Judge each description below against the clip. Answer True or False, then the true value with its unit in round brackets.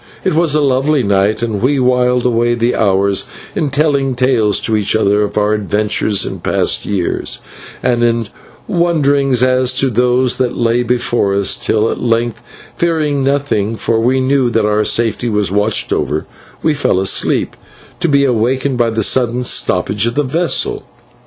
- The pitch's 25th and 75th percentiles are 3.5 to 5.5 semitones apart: True (4.0 semitones)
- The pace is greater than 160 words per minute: True (170 wpm)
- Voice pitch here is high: False (120 Hz)